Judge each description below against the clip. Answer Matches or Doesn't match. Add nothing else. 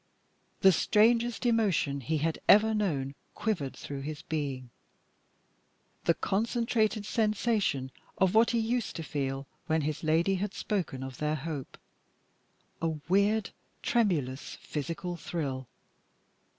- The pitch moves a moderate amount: Doesn't match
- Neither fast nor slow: Doesn't match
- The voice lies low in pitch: Doesn't match